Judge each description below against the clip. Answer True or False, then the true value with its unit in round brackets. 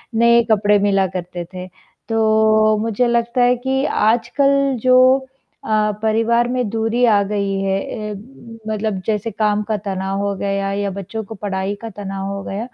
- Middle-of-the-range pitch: False (215 Hz)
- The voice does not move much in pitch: False (3.0 semitones)